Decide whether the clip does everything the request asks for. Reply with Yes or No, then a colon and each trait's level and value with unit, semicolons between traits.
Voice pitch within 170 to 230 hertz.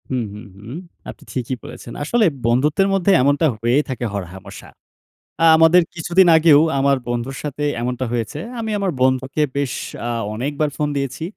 No: medium, 140 Hz